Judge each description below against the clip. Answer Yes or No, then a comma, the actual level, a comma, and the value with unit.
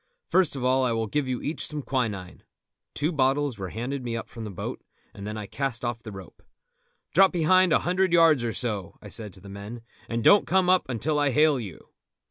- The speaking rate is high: Yes, fast, 225 wpm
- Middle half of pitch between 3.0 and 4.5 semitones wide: No, wide, 5.6 semitones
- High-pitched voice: No, low, 125 Hz